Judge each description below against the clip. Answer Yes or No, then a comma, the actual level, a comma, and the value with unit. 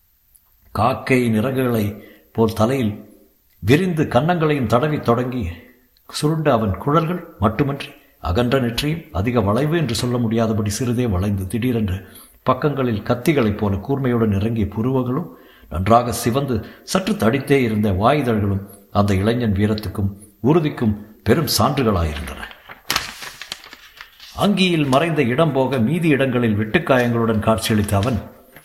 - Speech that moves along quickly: No, average, 105 wpm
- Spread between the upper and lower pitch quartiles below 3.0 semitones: No, average, 4.5 semitones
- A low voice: Yes, low, 115 Hz